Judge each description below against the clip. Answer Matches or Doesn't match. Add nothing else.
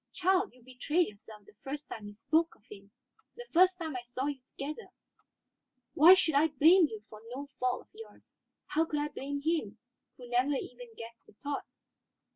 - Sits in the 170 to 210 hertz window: Doesn't match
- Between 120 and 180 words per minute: Doesn't match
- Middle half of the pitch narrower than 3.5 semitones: Doesn't match